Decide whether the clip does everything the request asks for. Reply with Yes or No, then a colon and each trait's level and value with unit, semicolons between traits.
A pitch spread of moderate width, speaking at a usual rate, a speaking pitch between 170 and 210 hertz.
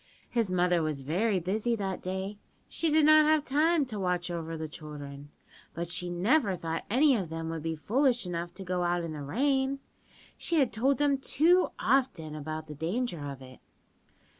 No: wide, 8.3 semitones; average, 190 wpm; medium, 185 Hz